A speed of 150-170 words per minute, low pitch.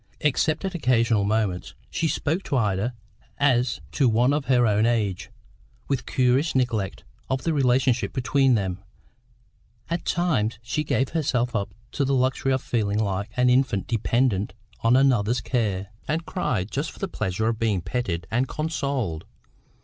Yes: average, 155 wpm; low, 125 Hz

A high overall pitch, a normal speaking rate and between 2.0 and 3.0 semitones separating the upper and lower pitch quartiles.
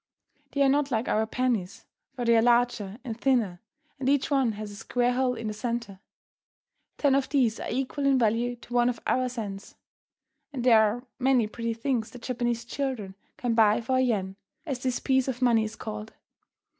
Yes: high, 240 Hz; average, 195 wpm; average, 2.7 semitones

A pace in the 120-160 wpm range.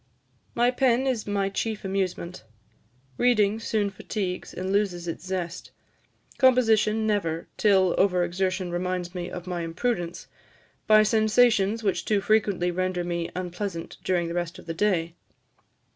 Yes: average, 140 wpm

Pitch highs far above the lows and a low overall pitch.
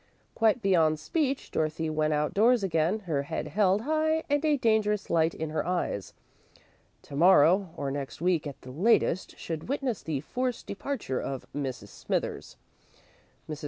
No: wide, 6.7 semitones; medium, 180 Hz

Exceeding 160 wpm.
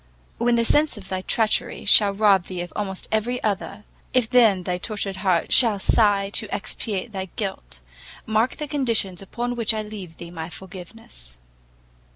Yes: average, 170 wpm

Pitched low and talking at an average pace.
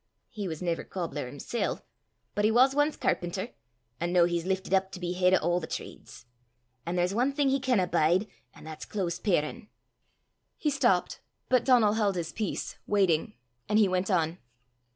No: medium, 185 Hz; average, 180 wpm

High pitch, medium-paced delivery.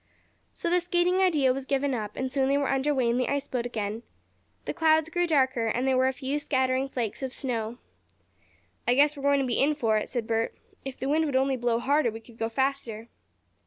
No: very high, 265 Hz; fast, 235 wpm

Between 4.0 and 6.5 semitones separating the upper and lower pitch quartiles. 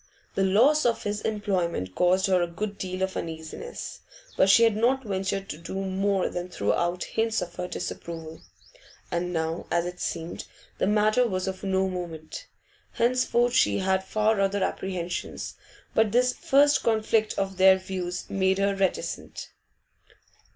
No: average, 3.2 semitones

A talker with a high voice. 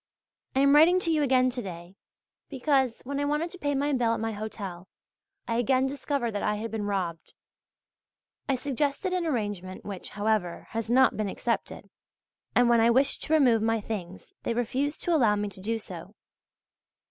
Yes: high, 235 Hz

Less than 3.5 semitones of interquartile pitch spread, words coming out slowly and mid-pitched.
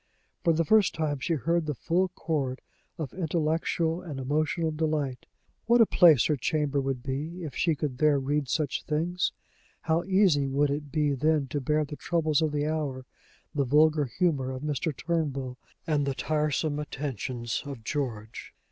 No: average, 2.8 semitones; average, 170 wpm; medium, 150 Hz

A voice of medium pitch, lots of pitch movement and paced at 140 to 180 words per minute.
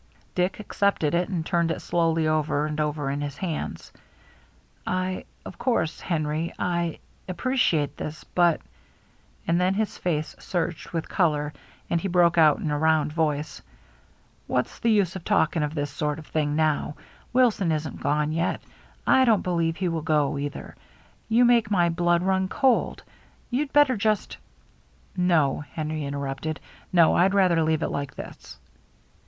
No: medium, 165 Hz; average, 3.5 semitones; average, 175 wpm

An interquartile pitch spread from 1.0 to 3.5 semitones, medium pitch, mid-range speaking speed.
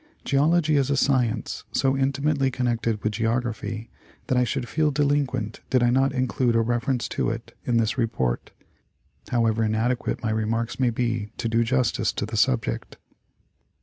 No: average, 2.8 semitones; low, 120 Hz; average, 160 wpm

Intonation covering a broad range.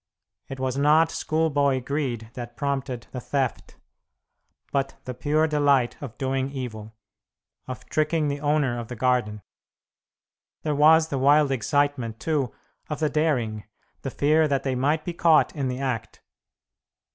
No: average, 3.1 semitones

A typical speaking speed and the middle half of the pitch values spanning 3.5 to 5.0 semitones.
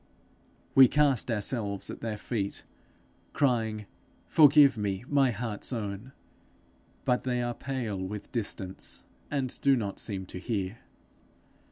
No: slow, 125 wpm; average, 4.3 semitones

